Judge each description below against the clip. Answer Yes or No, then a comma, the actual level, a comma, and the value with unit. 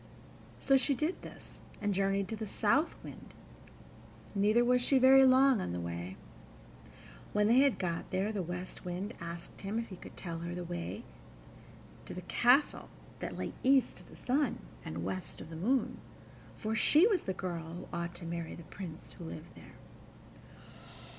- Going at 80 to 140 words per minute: No, average, 180 wpm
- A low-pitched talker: No, high, 195 Hz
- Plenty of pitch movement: Yes, wide, 6.6 semitones